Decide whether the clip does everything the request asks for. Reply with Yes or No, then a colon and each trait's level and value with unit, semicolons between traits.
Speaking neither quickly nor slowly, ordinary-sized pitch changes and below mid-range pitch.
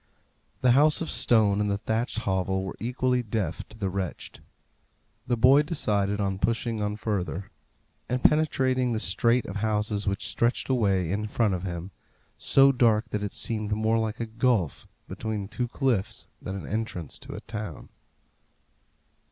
Yes: average, 160 wpm; average, 3.4 semitones; low, 110 Hz